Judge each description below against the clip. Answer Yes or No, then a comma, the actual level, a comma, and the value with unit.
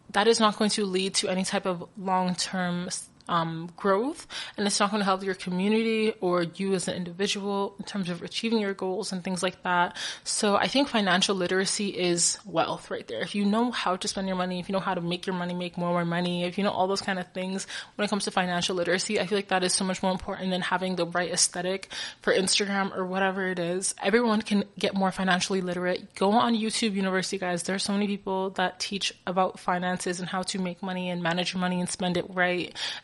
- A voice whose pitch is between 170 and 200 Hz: Yes, high, 190 Hz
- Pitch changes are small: Yes, narrow, 1.9 semitones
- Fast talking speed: Yes, fast, 240 wpm